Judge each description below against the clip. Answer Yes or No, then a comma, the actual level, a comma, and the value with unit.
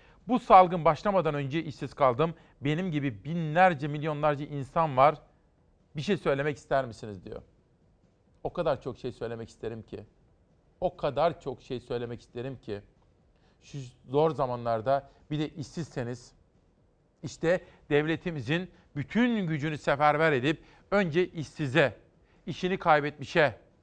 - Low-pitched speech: No, medium, 150 Hz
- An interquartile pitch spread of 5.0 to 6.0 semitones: No, average, 4.1 semitones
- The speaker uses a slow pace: No, average, 120 wpm